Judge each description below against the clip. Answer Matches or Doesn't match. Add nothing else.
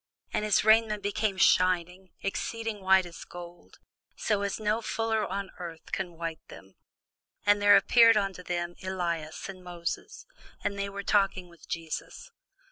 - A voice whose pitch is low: Doesn't match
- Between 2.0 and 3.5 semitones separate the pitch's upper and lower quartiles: Matches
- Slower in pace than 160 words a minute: Matches